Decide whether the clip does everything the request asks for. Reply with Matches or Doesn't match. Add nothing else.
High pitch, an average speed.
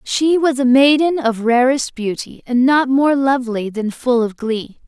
Matches